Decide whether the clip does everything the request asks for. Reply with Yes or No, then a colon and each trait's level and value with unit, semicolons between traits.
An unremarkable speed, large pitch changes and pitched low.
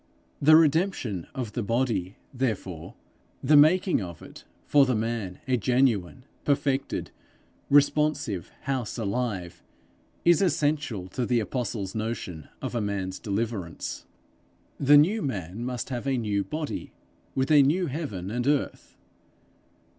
No: slow, 130 wpm; wide, 6.1 semitones; low, 125 Hz